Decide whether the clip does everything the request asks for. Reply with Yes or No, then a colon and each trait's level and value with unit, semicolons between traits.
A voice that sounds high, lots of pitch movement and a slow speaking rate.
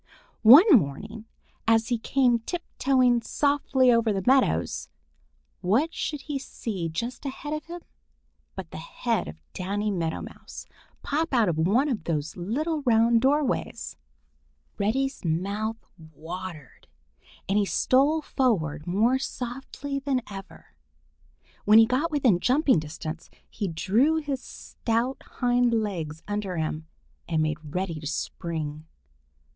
Yes: high, 225 Hz; wide, 7.4 semitones; slow, 130 wpm